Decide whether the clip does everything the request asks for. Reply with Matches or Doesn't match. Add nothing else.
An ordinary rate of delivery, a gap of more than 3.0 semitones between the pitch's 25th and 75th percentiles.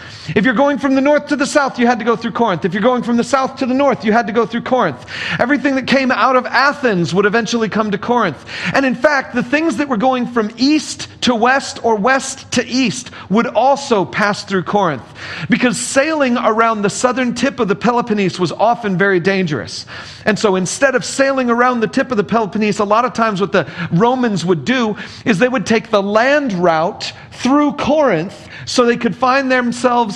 Doesn't match